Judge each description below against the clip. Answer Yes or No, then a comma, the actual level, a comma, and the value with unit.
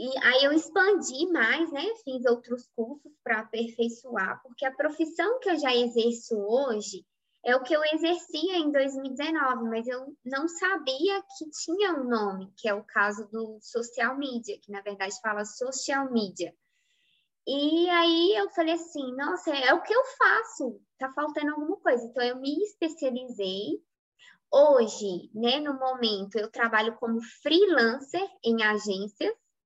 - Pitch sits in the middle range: No, very high, 265 Hz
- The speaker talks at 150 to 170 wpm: Yes, average, 155 wpm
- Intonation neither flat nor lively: No, wide, 6.3 semitones